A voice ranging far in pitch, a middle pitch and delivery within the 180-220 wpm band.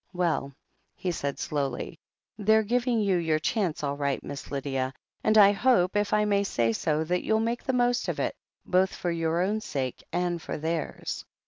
Yes: wide, 6.0 semitones; medium, 180 Hz; average, 190 wpm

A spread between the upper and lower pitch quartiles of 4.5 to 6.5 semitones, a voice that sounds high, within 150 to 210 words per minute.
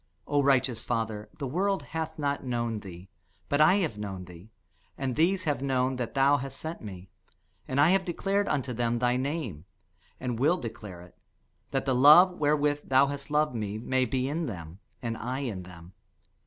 No: average, 4.8 semitones; low, 130 Hz; average, 185 wpm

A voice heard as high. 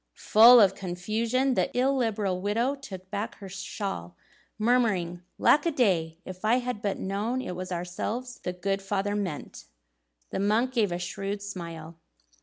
Yes: high, 200 Hz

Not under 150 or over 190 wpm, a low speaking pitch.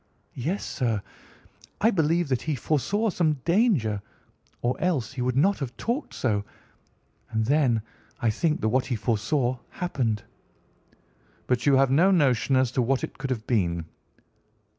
Yes: average, 155 wpm; low, 130 Hz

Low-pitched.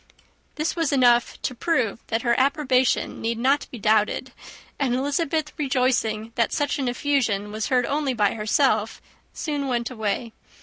No: very high, 250 Hz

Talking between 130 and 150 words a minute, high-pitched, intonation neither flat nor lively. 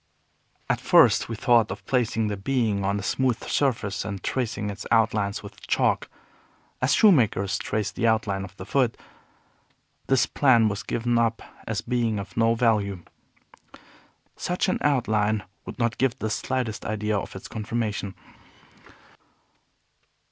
No: average, 140 wpm; low, 110 Hz; average, 3.1 semitones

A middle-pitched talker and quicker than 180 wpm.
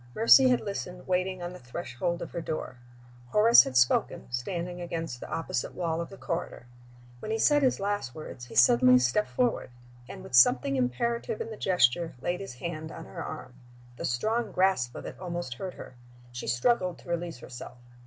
Yes: medium, 170 Hz; average, 190 wpm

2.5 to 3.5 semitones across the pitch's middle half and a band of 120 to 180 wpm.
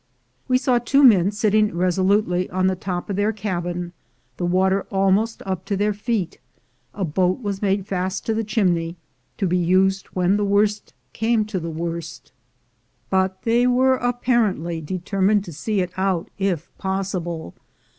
Yes: average, 2.8 semitones; average, 165 wpm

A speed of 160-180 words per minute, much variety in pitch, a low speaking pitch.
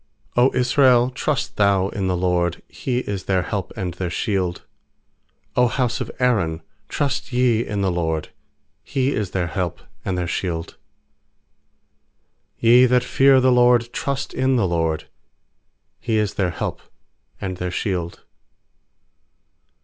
No: average, 140 wpm; wide, 5.7 semitones; low, 100 Hz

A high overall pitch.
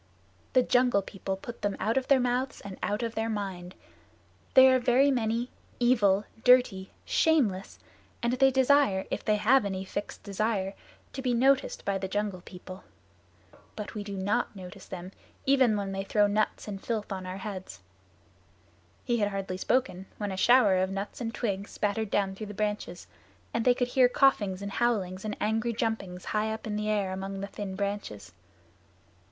Yes: high, 210 Hz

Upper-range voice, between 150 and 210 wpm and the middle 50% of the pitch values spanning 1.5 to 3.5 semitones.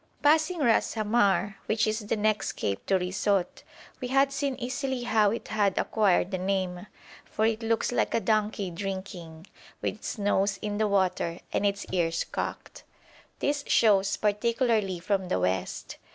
Yes: high, 205 Hz; average, 160 wpm; average, 3.2 semitones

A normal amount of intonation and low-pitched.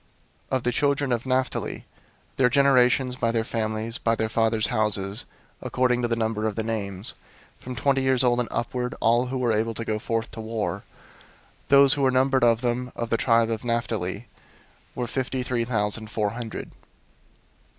No: narrow, 2.2 semitones; low, 115 Hz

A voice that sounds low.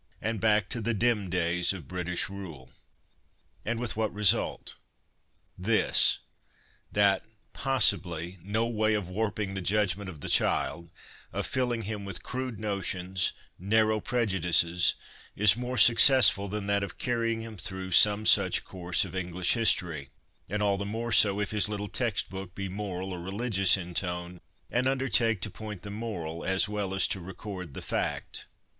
Yes: low, 100 Hz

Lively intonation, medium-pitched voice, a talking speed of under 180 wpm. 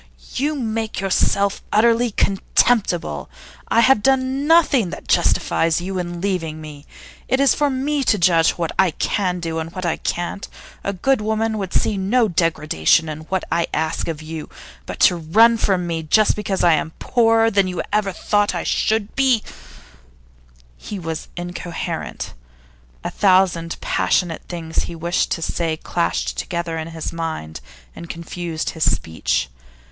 No: average, 5.0 semitones; medium, 180 Hz; average, 165 wpm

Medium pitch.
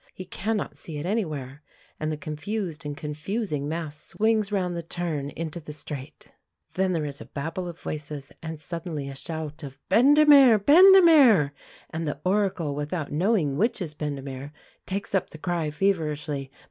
Yes: medium, 160 Hz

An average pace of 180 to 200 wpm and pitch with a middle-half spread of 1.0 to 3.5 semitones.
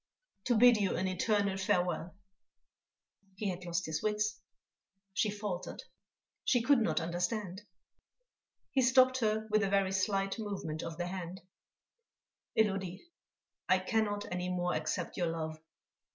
No: slow, 135 wpm; average, 3.2 semitones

